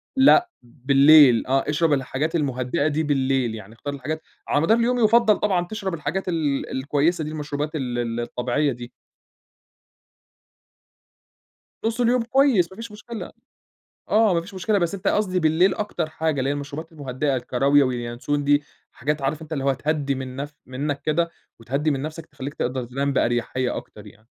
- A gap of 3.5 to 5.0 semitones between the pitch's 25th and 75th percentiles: Yes, average, 4.4 semitones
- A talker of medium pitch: Yes, medium, 145 Hz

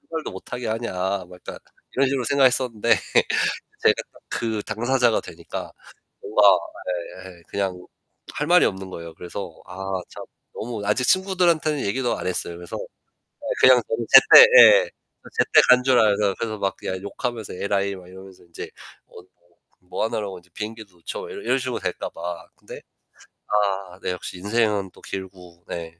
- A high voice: No, low, 105 Hz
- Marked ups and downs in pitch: No, average, 5.0 semitones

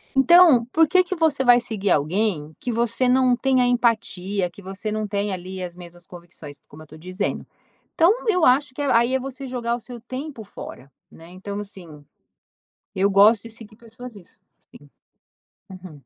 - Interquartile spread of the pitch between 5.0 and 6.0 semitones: Yes, wide, 5.5 semitones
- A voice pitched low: No, high, 220 Hz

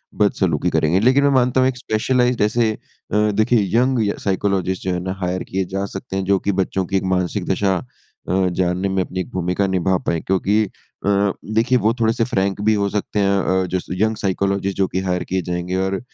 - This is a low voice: Yes, very low, 95 Hz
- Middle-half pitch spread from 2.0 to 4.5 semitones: Yes, average, 2.7 semitones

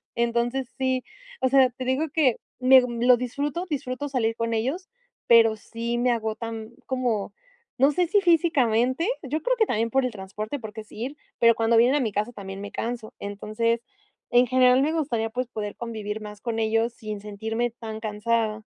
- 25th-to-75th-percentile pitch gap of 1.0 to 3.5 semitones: Yes, average, 2.9 semitones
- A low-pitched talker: No, high, 235 Hz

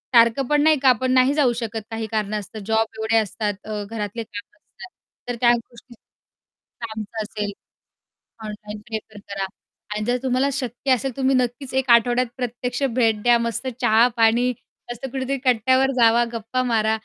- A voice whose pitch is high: Yes, high, 235 Hz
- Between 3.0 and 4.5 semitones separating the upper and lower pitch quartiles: No, narrow, 2.5 semitones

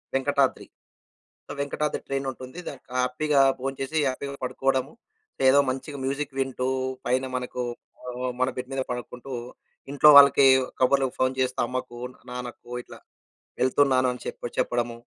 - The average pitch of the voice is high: No, low, 130 Hz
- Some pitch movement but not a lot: No, narrow, 1.5 semitones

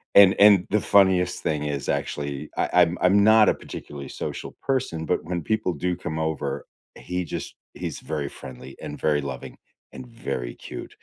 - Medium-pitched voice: No, very low, 85 Hz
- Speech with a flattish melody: No, average, 4.8 semitones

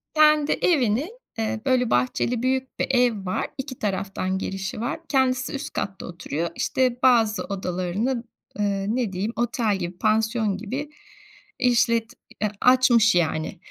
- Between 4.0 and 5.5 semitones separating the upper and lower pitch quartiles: Yes, average, 4.7 semitones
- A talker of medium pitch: No, high, 225 Hz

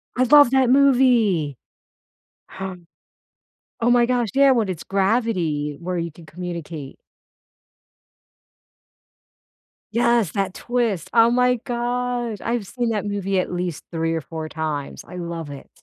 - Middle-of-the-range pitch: No, high, 200 Hz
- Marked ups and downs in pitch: Yes, wide, 6.2 semitones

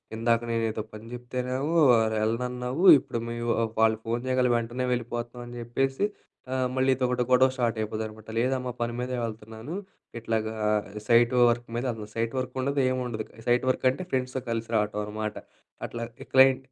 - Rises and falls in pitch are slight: Yes, narrow, 2.0 semitones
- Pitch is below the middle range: Yes, low, 120 Hz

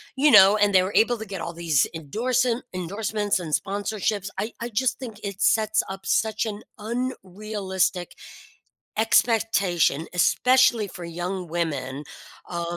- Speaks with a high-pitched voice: Yes, high, 200 Hz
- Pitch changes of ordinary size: Yes, average, 3.9 semitones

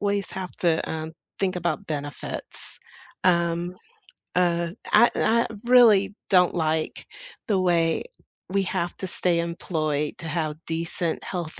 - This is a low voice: No, medium, 170 Hz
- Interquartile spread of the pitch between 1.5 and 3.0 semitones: Yes, average, 2.7 semitones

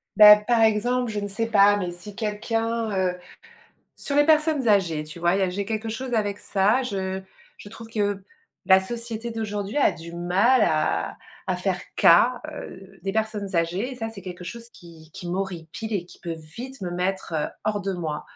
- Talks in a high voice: Yes, high, 205 Hz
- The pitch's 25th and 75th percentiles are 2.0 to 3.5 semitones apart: No, average, 3.9 semitones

